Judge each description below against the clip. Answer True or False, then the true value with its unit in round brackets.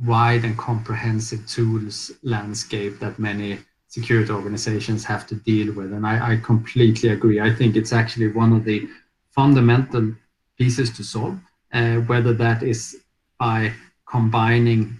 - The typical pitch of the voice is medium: False (115 Hz)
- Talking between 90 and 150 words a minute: True (140 wpm)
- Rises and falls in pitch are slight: True (1.5 semitones)